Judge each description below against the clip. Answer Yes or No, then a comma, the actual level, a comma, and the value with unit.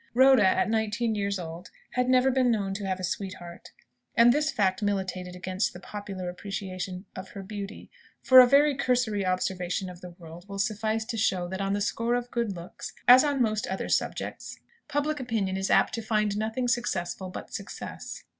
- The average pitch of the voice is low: No, high, 205 Hz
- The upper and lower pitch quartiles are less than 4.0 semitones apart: No, average, 4.3 semitones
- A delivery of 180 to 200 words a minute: Yes, average, 190 wpm